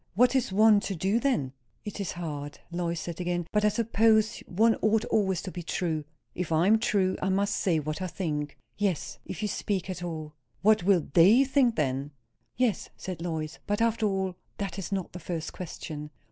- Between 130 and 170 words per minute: No, average, 200 wpm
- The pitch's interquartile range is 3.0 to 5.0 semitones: Yes, average, 4.1 semitones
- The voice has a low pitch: No, medium, 185 Hz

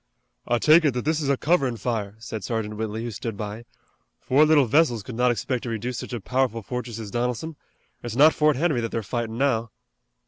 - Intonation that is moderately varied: Yes, average, 3.5 semitones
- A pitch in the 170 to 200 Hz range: No, low, 120 Hz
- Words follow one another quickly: Yes, fast, 215 wpm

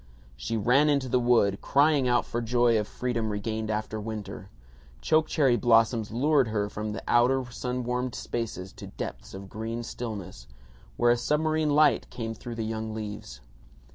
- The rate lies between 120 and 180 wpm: Yes, average, 170 wpm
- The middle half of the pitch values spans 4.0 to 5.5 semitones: No, average, 2.7 semitones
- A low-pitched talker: Yes, low, 115 Hz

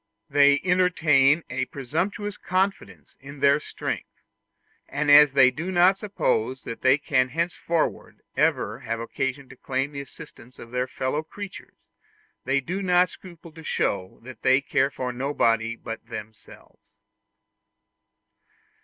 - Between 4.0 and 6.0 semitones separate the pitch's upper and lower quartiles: Yes, average, 4.7 semitones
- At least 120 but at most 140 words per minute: Yes, slow, 135 wpm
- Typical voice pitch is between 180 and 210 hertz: No, medium, 140 Hz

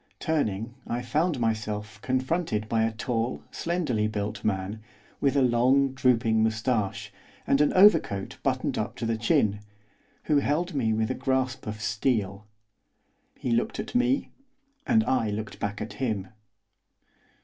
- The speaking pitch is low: Yes, low, 115 Hz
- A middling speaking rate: Yes, average, 145 wpm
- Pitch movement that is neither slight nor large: Yes, average, 3.7 semitones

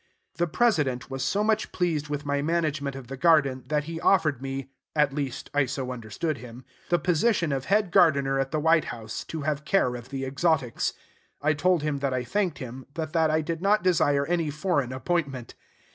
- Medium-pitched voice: Yes, medium, 150 Hz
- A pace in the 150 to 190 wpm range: No, average, 200 wpm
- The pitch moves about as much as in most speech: Yes, average, 3.7 semitones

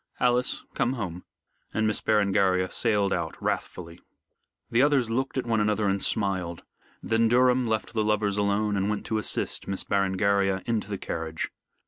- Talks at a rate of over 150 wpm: Yes, average, 160 wpm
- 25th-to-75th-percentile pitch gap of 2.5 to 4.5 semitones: Yes, average, 2.8 semitones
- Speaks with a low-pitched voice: Yes, low, 105 Hz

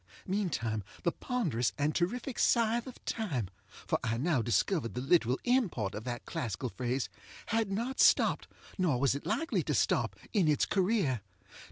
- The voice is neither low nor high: Yes, medium, 160 Hz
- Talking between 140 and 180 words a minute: Yes, average, 160 wpm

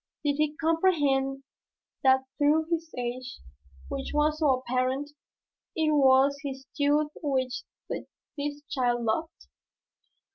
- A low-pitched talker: No, very high, 285 Hz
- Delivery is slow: Yes, slow, 110 wpm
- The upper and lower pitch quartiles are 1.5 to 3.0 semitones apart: Yes, narrow, 2.5 semitones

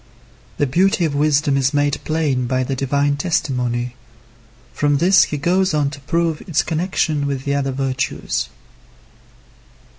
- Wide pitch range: No, average, 2.8 semitones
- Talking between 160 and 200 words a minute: No, average, 145 wpm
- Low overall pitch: No, medium, 145 Hz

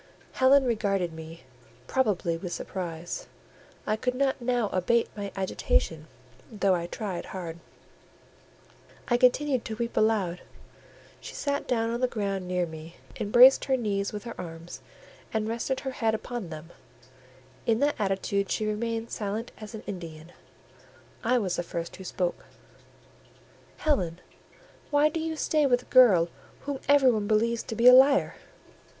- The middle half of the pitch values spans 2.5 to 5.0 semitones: No, wide, 5.5 semitones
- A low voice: No, high, 215 Hz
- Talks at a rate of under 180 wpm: Yes, average, 150 wpm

